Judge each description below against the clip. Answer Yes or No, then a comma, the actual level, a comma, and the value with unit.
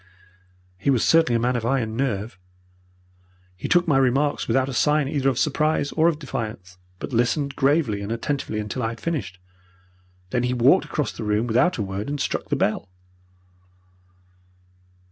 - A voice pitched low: Yes, low, 125 Hz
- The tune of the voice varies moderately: Yes, average, 4.6 semitones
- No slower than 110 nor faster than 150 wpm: No, average, 170 wpm